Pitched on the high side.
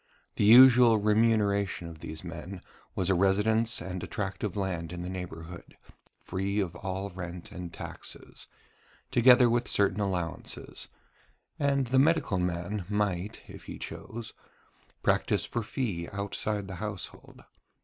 No: low, 100 Hz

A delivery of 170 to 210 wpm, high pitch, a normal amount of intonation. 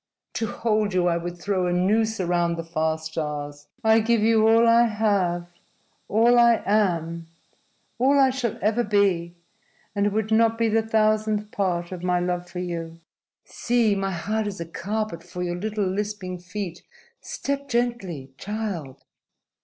No: average, 160 wpm; high, 200 Hz; average, 4.1 semitones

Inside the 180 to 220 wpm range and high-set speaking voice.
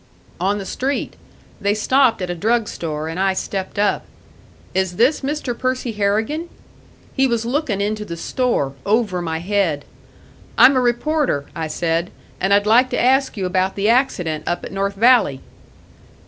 No: average, 165 wpm; high, 205 Hz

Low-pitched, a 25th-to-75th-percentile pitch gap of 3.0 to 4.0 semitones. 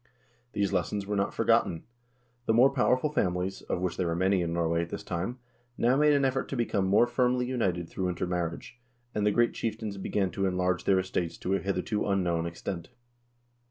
No: very low, 95 Hz; average, 4.9 semitones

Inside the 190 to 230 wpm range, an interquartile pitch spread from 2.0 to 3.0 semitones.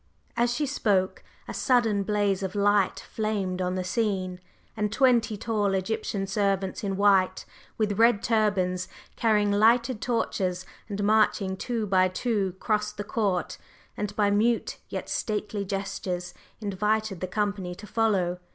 No: average, 140 wpm; narrow, 2.4 semitones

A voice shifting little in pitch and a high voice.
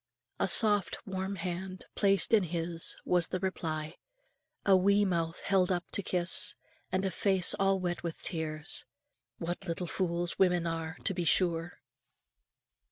No: narrow, 2.2 semitones; medium, 180 Hz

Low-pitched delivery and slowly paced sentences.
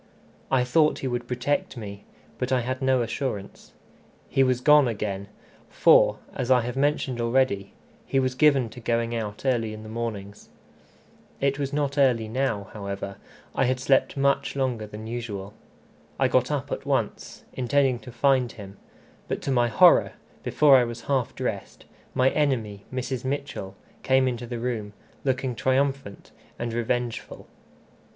No: low, 125 Hz; average, 160 wpm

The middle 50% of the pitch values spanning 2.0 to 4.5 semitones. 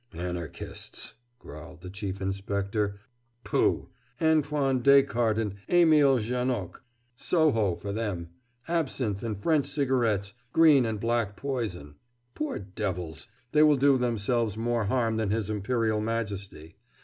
No: average, 4.9 semitones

